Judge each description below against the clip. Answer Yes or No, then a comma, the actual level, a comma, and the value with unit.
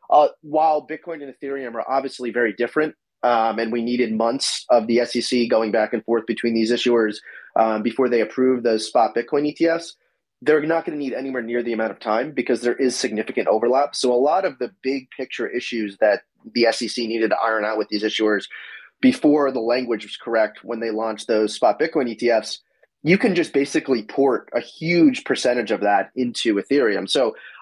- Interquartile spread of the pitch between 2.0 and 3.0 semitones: No, average, 3.5 semitones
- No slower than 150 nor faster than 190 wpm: No, average, 200 wpm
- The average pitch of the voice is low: Yes, low, 120 Hz